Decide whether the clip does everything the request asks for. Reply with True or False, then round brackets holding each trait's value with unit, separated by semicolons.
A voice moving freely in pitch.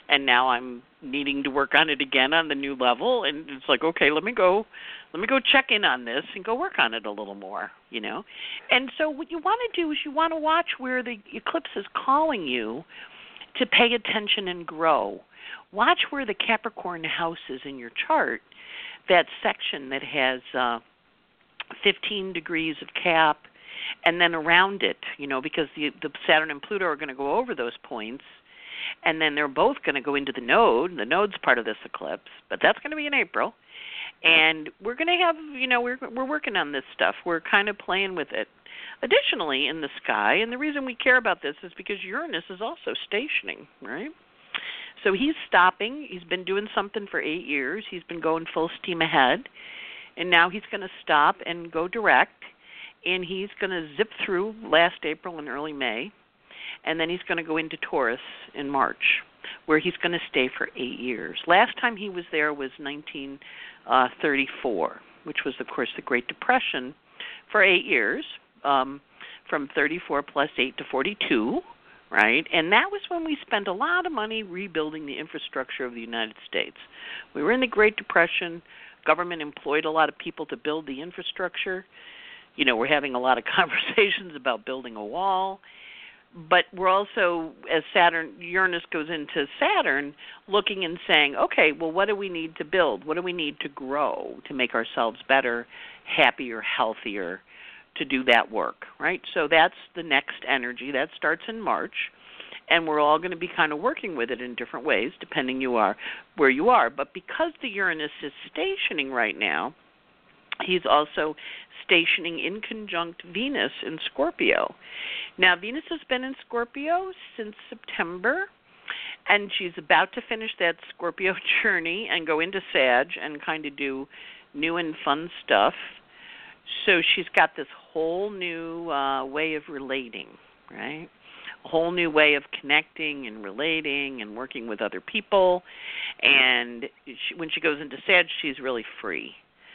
True (6.7 semitones)